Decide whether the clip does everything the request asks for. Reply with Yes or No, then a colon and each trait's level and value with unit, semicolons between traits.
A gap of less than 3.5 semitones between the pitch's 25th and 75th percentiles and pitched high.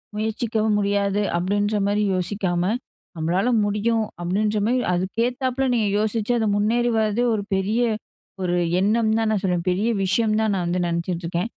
Yes: average, 3.0 semitones; high, 210 Hz